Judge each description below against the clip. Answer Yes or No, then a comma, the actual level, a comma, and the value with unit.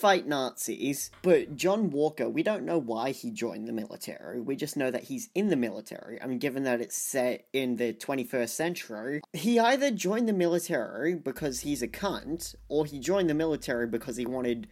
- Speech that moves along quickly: No, average, 195 wpm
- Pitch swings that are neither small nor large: No, wide, 6.0 semitones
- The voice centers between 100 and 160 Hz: Yes, medium, 140 Hz